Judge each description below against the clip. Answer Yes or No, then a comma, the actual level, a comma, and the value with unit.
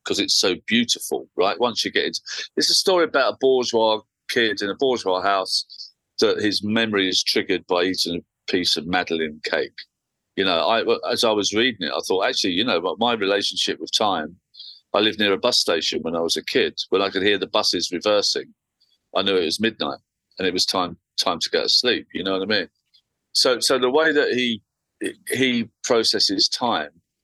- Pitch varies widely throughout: Yes, wide, 5.9 semitones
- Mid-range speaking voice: No, low, 105 Hz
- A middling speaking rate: No, fast, 210 wpm